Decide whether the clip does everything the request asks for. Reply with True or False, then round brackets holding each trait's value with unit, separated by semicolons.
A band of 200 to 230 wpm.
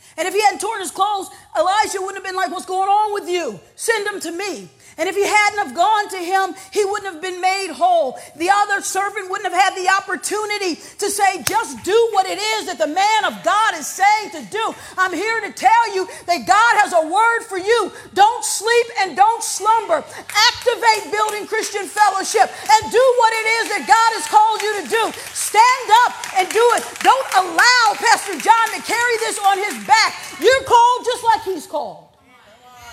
True (205 wpm)